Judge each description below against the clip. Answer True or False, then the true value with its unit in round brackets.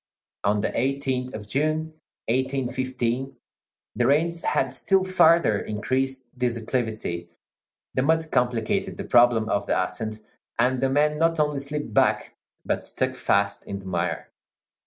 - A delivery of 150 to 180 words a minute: False (140 wpm)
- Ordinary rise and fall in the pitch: True (4.6 semitones)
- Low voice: True (130 Hz)